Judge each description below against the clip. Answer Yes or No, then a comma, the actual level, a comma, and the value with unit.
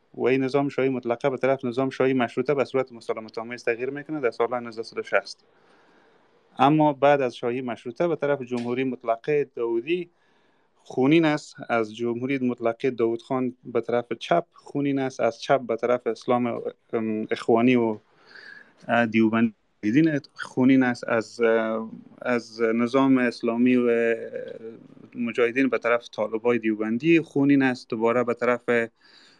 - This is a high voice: No, low, 125 Hz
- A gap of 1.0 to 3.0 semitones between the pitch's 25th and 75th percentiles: Yes, narrow, 2.6 semitones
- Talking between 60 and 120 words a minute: No, average, 135 wpm